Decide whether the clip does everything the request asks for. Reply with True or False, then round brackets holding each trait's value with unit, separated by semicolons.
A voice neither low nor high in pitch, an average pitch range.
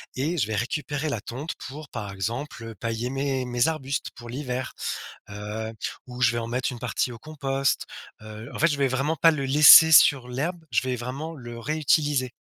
False (130 Hz; 3.7 semitones)